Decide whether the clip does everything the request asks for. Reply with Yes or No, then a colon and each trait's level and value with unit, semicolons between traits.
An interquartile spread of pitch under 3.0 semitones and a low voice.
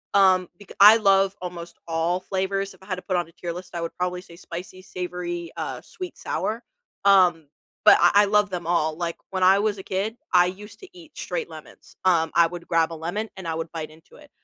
No: narrow, 2.6 semitones; medium, 180 Hz